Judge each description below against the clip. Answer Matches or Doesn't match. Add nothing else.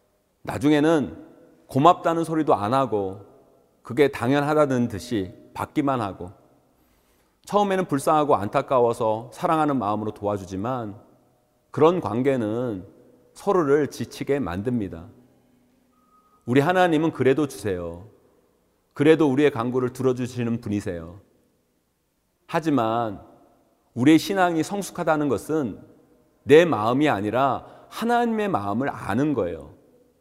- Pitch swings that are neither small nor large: Doesn't match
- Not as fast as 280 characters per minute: Matches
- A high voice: Doesn't match